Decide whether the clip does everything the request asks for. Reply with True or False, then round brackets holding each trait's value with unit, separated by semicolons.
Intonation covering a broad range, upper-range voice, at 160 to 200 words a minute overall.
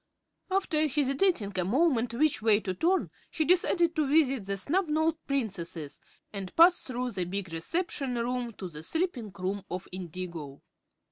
False (8.9 semitones; 245 Hz; 150 wpm)